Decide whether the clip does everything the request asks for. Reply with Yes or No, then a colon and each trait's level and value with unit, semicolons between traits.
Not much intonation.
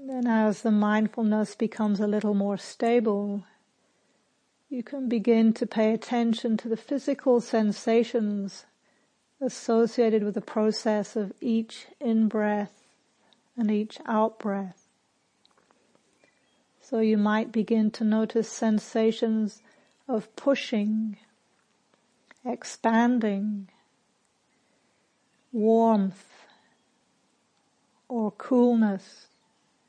Yes: narrow, 2.1 semitones